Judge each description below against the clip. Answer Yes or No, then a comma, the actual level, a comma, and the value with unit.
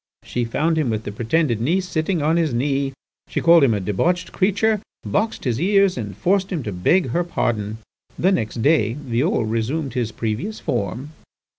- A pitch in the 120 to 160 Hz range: Yes, medium, 140 Hz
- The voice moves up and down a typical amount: No, wide, 7.5 semitones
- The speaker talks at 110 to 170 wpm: No, average, 180 wpm